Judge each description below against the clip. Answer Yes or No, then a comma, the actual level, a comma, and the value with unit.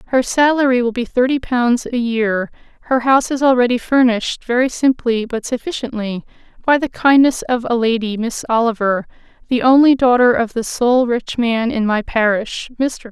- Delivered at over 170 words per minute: No, average, 165 wpm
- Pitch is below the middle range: No, high, 240 Hz